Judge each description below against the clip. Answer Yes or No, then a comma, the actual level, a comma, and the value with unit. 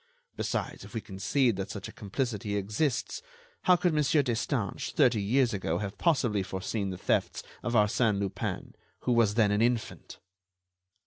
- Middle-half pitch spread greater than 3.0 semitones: Yes, average, 3.8 semitones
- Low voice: Yes, low, 110 Hz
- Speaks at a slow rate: No, average, 155 wpm